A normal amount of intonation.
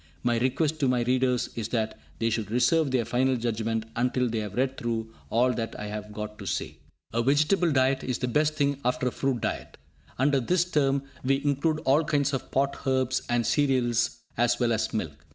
Yes: average, 3.1 semitones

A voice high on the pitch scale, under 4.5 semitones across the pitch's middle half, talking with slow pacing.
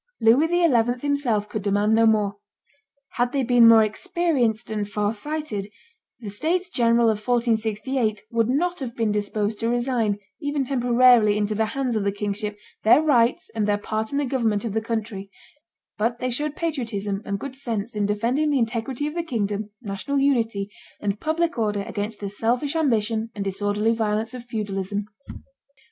No: high, 225 Hz; average, 3.6 semitones; average, 170 wpm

